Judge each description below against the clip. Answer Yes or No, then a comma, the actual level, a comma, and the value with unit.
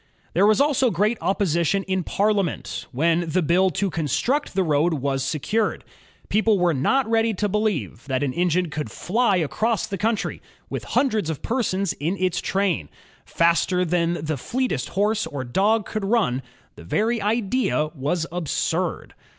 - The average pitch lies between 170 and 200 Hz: Yes, medium, 185 Hz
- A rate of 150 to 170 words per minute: Yes, average, 160 wpm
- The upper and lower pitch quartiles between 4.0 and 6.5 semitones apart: Yes, average, 5.1 semitones